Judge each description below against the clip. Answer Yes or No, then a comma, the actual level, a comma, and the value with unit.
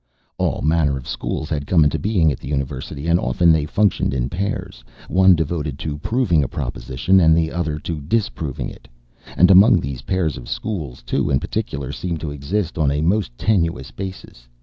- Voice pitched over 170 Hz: No, very low, 80 Hz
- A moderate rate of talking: Yes, average, 190 wpm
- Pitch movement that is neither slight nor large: Yes, average, 4.6 semitones